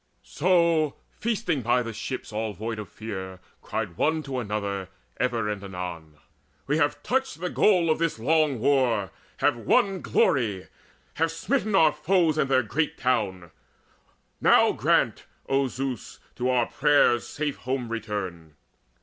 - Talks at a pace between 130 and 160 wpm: Yes, average, 145 wpm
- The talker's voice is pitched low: Yes, low, 130 Hz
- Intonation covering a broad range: Yes, wide, 6.9 semitones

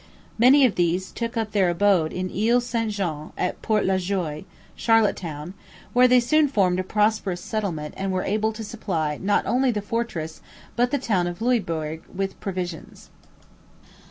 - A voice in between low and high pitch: No, high, 200 Hz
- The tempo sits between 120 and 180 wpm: Yes, average, 165 wpm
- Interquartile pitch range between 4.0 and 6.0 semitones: Yes, average, 4.5 semitones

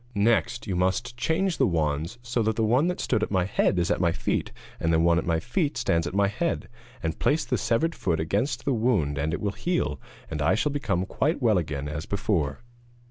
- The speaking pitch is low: Yes, low, 100 Hz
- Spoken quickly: Yes, fast, 230 wpm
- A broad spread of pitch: Yes, wide, 6.5 semitones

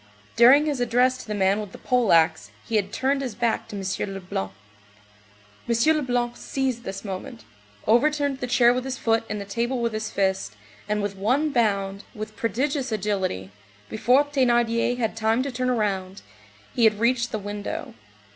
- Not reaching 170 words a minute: No, average, 175 wpm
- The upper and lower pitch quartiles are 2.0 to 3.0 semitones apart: No, average, 3.8 semitones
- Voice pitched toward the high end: Yes, high, 230 Hz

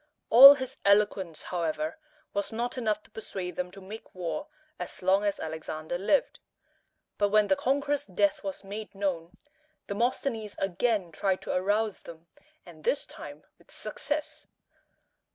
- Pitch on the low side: No, high, 200 Hz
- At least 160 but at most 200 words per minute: No, average, 145 wpm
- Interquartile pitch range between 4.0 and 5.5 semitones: No, average, 3.6 semitones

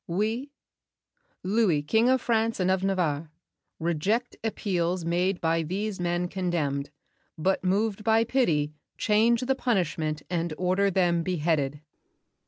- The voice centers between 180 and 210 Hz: Yes, medium, 185 Hz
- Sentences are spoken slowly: Yes, slow, 125 wpm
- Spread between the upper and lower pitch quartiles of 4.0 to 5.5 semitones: Yes, average, 4.5 semitones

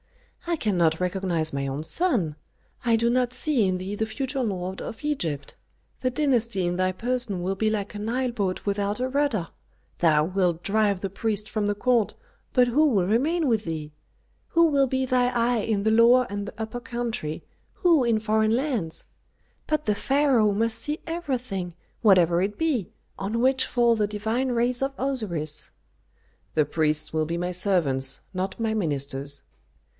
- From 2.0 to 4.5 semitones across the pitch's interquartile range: No, wide, 5.6 semitones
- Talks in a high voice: Yes, high, 215 Hz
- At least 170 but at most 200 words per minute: Yes, average, 175 wpm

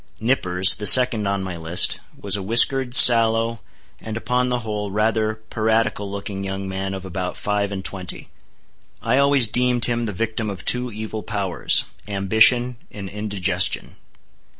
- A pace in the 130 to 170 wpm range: Yes, average, 150 wpm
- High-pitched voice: No, low, 105 Hz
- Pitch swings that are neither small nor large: Yes, average, 3.0 semitones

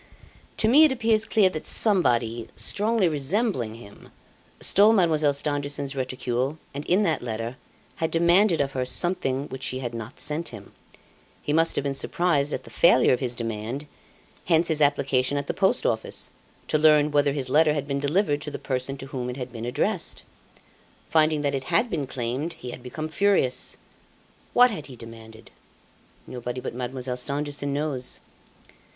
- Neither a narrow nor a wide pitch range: Yes, average, 4.5 semitones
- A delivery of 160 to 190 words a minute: Yes, average, 170 wpm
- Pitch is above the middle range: No, medium, 145 Hz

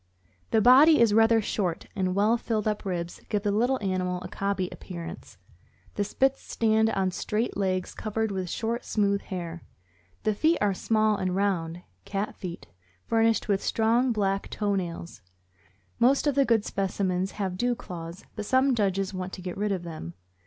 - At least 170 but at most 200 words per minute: Yes, average, 175 wpm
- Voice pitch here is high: Yes, high, 200 Hz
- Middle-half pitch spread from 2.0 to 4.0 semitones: Yes, average, 3.2 semitones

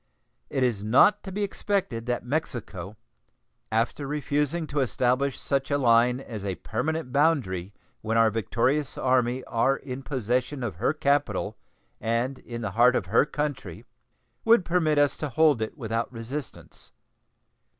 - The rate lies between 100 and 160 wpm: Yes, average, 150 wpm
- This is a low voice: Yes, low, 130 Hz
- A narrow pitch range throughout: No, average, 4.2 semitones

